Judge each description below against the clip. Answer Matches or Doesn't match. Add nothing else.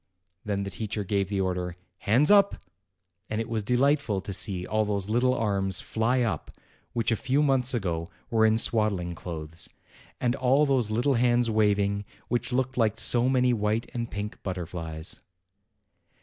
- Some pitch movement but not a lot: Matches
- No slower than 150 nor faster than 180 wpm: Matches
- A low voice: Matches